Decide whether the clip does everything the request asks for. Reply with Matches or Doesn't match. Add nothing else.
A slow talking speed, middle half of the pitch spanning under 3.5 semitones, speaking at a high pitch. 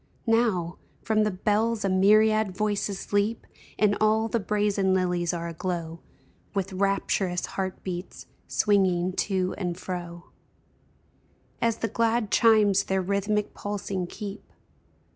Matches